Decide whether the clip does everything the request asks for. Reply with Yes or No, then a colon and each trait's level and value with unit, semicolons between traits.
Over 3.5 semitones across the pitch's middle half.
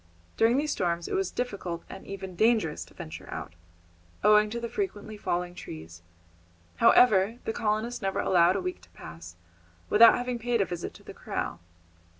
Yes: average, 4.9 semitones